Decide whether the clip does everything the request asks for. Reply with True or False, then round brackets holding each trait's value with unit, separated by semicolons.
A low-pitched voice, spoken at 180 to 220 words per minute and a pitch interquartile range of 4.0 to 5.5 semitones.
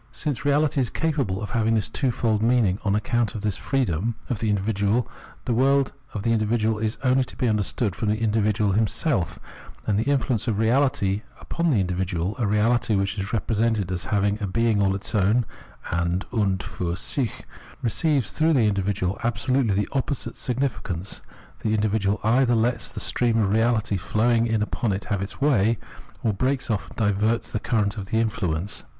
False (110 Hz; 185 wpm; 3.1 semitones)